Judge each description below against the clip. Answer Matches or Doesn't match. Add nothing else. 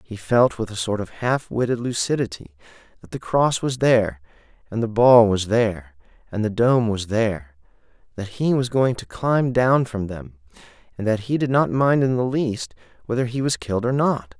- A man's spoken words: Matches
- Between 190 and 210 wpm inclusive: Matches